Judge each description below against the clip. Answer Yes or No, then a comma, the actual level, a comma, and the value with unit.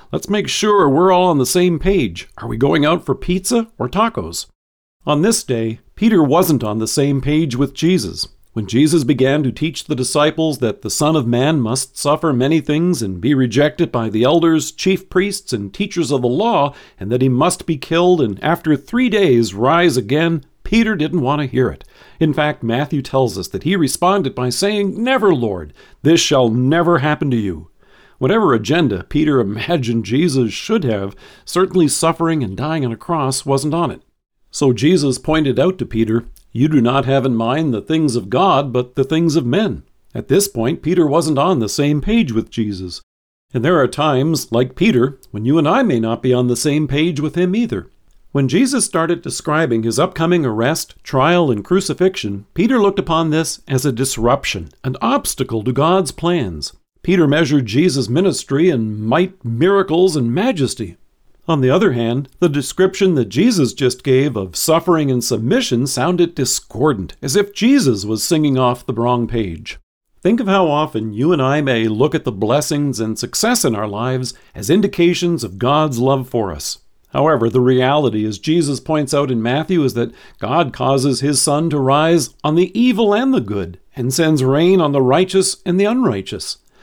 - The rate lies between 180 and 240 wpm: Yes, average, 190 wpm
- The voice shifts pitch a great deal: Yes, wide, 5.7 semitones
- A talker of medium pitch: Yes, medium, 145 Hz